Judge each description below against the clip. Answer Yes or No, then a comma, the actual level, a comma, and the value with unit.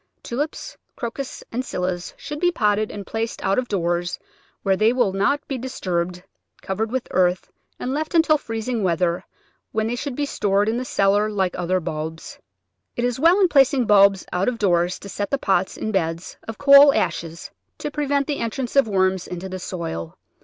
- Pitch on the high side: Yes, high, 210 Hz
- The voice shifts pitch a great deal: Yes, wide, 6.0 semitones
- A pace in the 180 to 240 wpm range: Yes, average, 190 wpm